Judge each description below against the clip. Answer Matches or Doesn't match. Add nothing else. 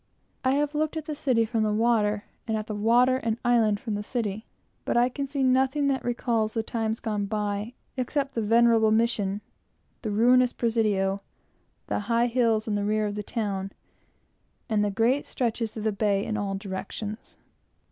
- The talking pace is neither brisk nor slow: Matches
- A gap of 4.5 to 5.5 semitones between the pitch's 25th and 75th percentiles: Doesn't match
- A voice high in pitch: Matches